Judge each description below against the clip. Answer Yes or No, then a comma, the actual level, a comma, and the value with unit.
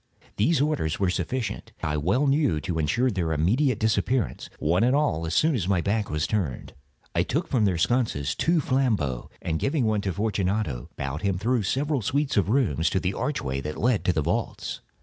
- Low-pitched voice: Yes, low, 100 Hz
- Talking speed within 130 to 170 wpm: No, average, 195 wpm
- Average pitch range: No, wide, 7.9 semitones